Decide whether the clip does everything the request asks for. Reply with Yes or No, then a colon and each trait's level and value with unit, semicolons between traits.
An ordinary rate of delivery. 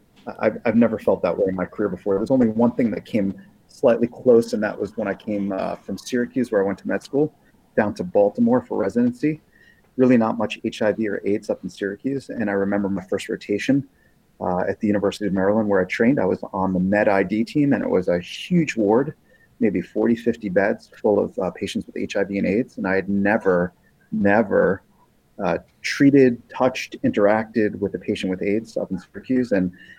No: fast, 210 wpm